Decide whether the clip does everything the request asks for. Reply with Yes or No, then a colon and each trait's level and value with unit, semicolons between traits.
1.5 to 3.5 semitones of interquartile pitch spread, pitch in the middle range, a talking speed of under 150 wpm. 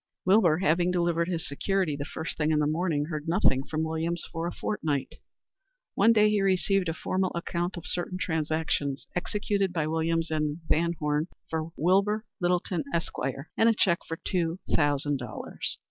No: average, 2.8 semitones; medium, 170 Hz; average, 170 wpm